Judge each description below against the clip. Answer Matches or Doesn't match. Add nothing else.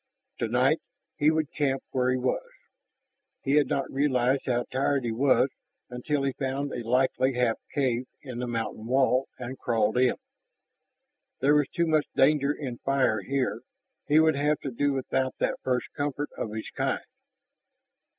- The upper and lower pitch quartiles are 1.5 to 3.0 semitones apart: Matches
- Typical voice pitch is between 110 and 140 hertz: Matches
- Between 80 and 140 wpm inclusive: Doesn't match